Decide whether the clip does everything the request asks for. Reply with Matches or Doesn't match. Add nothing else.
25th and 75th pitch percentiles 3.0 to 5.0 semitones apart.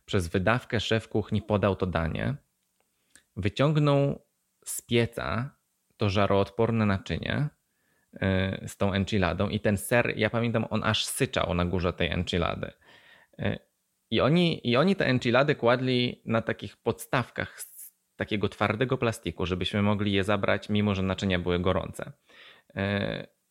Matches